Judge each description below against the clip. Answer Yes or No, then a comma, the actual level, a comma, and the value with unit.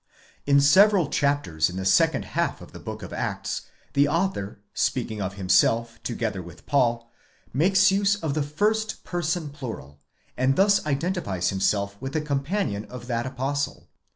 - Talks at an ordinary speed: Yes, average, 160 wpm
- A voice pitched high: No, medium, 140 Hz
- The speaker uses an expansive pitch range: Yes, wide, 7.4 semitones